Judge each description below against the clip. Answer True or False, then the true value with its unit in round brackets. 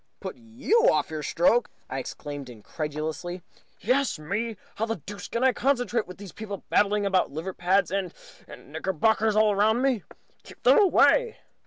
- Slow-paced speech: False (160 wpm)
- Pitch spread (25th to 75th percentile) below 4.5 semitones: False (5.4 semitones)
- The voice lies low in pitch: False (205 Hz)